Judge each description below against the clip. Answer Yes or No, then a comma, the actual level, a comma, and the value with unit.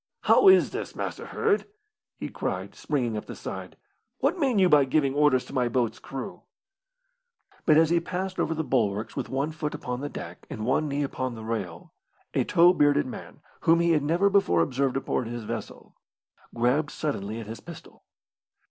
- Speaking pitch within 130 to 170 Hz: Yes, medium, 140 Hz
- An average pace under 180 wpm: No, average, 185 wpm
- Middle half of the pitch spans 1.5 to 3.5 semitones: No, average, 5.3 semitones